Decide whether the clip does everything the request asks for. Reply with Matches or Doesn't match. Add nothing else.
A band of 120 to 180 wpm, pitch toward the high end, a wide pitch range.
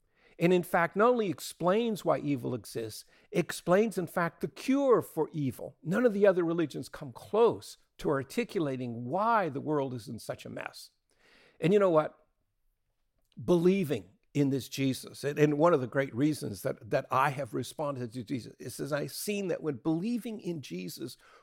Doesn't match